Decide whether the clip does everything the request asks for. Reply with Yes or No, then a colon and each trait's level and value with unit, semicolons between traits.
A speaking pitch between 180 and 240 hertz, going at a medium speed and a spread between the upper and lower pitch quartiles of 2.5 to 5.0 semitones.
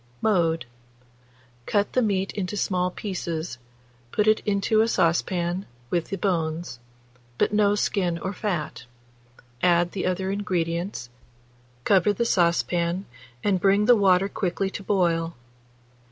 No: medium, 185 Hz; slow, 125 wpm; average, 2.9 semitones